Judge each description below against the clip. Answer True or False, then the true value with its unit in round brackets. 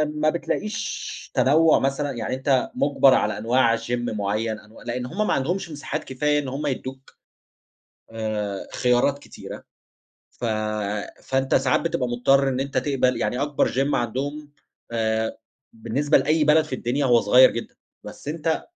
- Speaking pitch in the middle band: False (130 Hz)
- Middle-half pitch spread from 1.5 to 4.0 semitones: True (3.6 semitones)